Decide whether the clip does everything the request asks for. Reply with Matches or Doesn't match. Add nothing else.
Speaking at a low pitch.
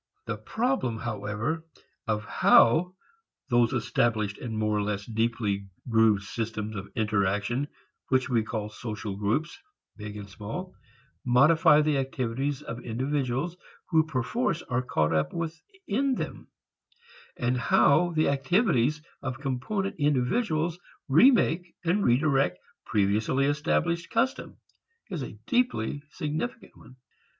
Matches